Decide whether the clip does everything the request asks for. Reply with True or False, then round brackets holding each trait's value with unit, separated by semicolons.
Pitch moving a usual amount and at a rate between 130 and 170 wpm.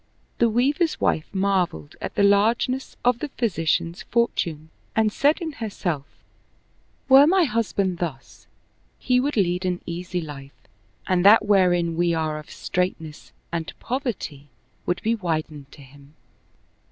False (6.3 semitones; 140 wpm)